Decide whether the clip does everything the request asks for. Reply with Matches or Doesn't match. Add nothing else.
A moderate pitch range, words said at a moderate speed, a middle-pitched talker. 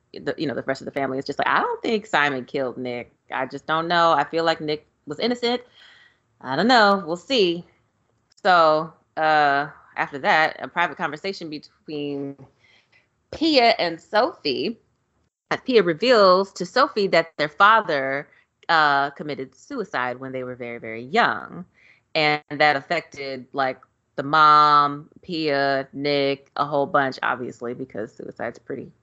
Matches